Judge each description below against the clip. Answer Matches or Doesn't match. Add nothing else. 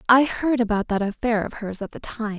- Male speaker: Doesn't match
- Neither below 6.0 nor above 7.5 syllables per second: Doesn't match